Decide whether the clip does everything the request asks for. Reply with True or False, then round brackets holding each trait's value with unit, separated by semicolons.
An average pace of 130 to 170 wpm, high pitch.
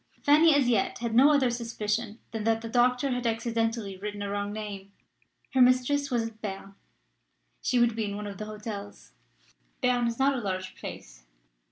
False (185 wpm; 225 Hz)